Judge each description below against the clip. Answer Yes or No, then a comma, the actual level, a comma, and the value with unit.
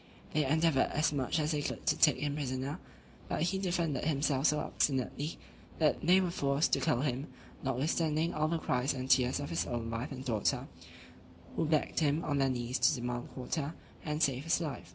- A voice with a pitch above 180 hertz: No, medium, 145 Hz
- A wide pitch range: No, average, 3.3 semitones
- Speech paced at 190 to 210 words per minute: Yes, average, 195 wpm